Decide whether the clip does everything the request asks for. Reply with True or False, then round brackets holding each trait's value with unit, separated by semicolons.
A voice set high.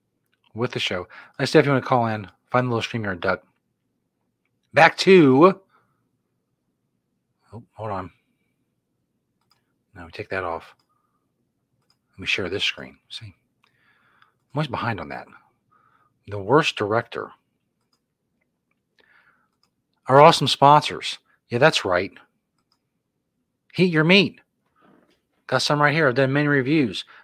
False (135 Hz)